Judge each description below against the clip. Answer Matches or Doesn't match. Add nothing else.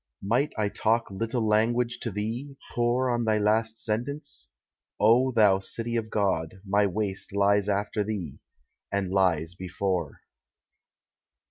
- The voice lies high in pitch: Doesn't match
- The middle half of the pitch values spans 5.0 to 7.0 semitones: Doesn't match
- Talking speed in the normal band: Doesn't match